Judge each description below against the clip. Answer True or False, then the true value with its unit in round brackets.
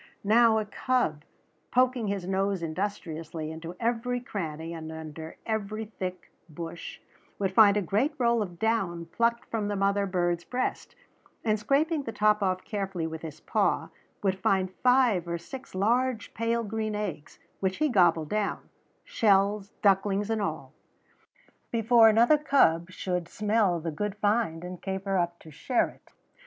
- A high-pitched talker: True (200 Hz)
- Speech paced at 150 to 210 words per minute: True (155 wpm)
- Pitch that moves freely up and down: False (4.5 semitones)